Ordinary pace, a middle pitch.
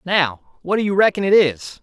No: fast, 230 wpm; medium, 175 Hz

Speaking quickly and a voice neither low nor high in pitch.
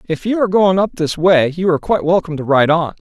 Yes: fast, 275 wpm; medium, 170 Hz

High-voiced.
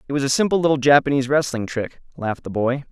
No: low, 135 Hz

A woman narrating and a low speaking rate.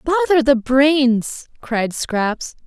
Yes: female; slow, 115 wpm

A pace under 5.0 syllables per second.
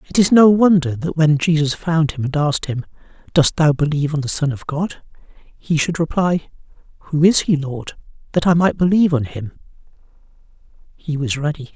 No: 5.4 syllables/s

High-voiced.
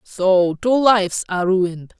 Yes: high, 195 Hz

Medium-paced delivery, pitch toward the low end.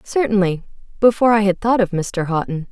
No: average, 155 wpm; high, 200 Hz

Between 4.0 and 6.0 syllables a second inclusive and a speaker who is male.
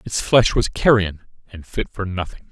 Yes: 4.7 syllables/s; male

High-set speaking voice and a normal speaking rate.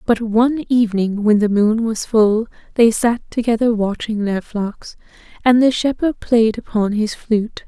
Yes: high, 225 Hz; average, 165 wpm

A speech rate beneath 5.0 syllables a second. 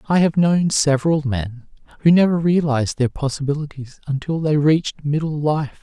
No: 5.1 syllables/s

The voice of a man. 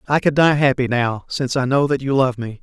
Yes: male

